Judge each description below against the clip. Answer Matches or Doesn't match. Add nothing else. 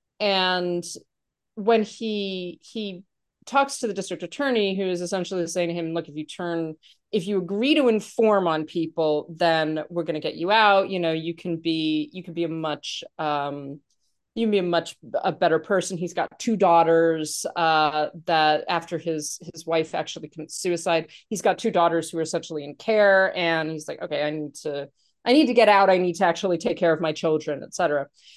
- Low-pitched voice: Doesn't match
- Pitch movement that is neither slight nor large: Matches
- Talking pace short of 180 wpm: Doesn't match